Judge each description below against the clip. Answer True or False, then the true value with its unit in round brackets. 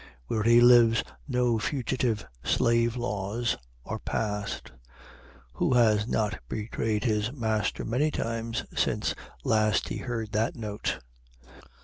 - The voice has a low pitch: True (115 Hz)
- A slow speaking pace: True (115 wpm)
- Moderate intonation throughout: False (2.0 semitones)